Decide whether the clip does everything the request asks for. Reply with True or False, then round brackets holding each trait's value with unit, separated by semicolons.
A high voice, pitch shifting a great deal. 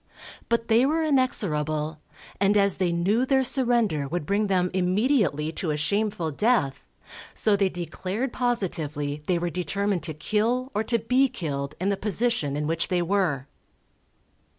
True (195 Hz; 6.4 semitones)